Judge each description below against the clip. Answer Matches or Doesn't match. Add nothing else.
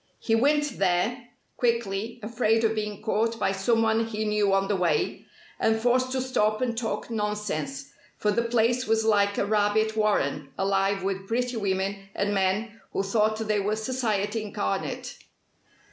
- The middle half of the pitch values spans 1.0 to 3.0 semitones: Matches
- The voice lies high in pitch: Matches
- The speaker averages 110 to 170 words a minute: Matches